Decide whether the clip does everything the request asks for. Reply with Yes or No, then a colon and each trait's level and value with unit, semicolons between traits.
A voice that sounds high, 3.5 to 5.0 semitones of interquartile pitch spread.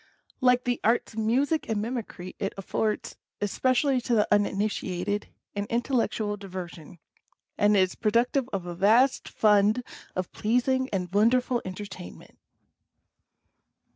Yes: high, 215 Hz; average, 3.8 semitones